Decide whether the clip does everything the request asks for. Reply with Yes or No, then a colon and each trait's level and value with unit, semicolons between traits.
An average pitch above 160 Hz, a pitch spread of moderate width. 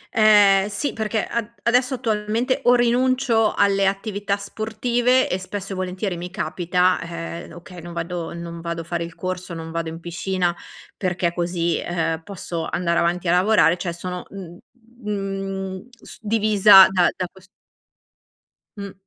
Yes: high, 190 Hz; average, 3.5 semitones